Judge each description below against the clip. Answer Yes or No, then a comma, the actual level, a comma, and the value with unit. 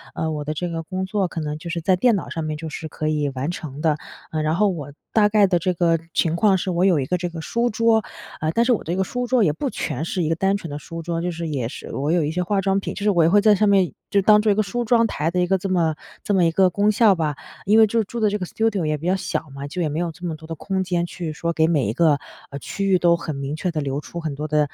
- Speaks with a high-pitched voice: No, medium, 175 Hz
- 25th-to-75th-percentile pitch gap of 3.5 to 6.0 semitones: Yes, average, 4.0 semitones